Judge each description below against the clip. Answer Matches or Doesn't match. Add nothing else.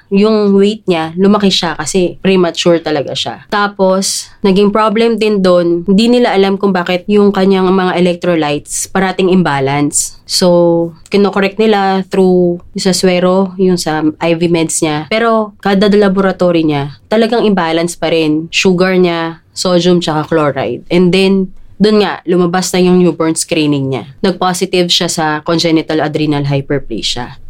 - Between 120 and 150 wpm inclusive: Matches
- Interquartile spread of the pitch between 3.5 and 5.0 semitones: Doesn't match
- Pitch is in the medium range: Matches